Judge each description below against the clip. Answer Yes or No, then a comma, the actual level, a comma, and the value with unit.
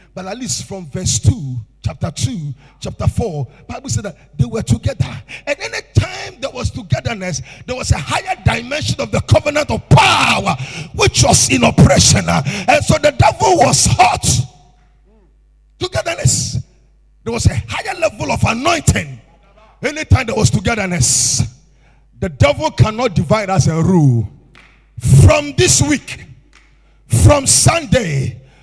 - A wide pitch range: Yes, wide, 7.6 semitones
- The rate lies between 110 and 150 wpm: Yes, average, 140 wpm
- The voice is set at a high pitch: No, medium, 140 Hz